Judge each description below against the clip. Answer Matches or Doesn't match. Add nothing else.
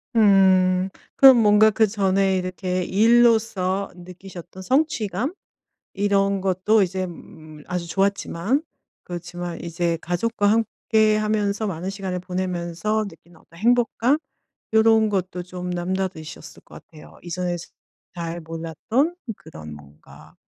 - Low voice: Doesn't match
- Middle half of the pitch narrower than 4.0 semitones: Matches